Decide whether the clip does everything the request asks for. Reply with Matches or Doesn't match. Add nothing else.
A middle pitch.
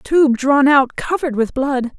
Doesn't match